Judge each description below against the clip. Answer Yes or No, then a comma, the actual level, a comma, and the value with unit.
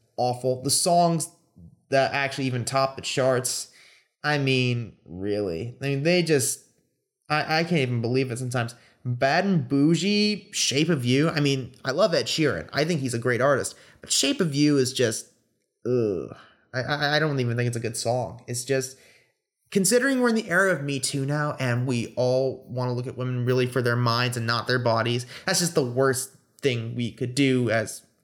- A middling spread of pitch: Yes, average, 3.4 semitones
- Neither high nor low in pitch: No, low, 130 Hz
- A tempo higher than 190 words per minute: Yes, average, 200 wpm